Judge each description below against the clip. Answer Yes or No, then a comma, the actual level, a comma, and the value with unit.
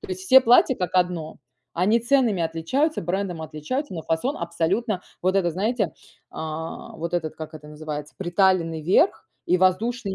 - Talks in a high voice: No, medium, 180 Hz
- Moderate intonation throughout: No, wide, 5.9 semitones